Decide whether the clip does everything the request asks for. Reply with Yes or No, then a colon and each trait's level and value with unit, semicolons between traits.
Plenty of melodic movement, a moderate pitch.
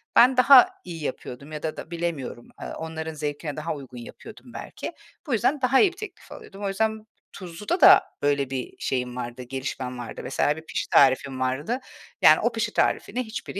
Yes: wide, 8.5 semitones; medium, 155 Hz